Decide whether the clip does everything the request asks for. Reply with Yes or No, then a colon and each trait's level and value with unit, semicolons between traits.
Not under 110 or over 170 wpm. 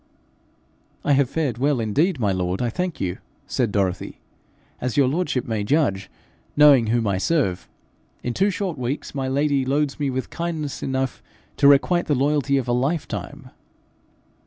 Yes: average, 160 wpm